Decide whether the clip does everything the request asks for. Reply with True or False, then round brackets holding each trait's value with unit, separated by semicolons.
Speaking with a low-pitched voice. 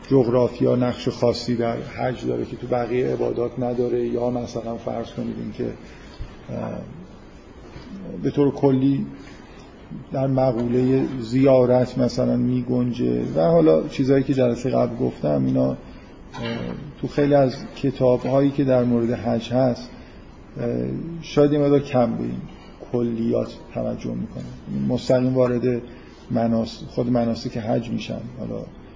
True (120 Hz)